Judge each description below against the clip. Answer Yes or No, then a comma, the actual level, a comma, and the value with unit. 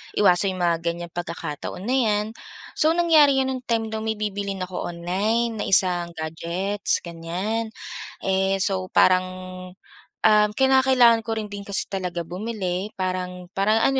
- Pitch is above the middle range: Yes, high, 195 Hz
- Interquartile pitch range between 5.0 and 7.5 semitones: No, average, 3.8 semitones